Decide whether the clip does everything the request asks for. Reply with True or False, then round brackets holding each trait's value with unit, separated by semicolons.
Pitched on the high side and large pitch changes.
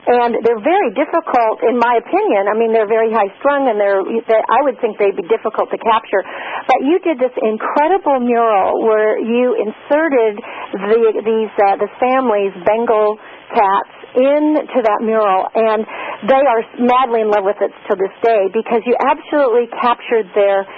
False (230 Hz; 3.5 semitones)